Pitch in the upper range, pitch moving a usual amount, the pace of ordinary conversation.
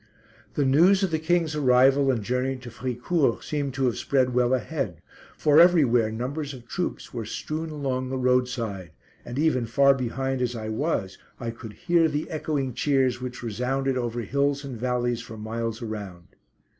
No: low, 130 Hz; average, 3.3 semitones; average, 170 wpm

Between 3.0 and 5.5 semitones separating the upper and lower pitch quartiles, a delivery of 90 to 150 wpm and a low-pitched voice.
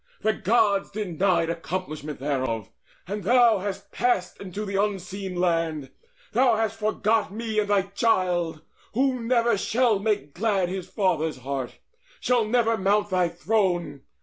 No: average, 4.1 semitones; average, 140 wpm; high, 195 Hz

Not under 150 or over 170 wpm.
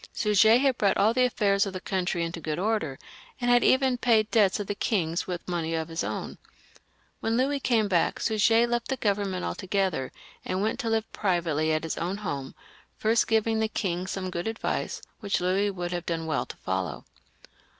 No: average, 195 wpm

